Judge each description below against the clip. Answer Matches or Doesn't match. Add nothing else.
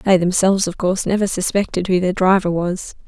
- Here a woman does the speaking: Matches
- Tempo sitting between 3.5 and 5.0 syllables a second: Doesn't match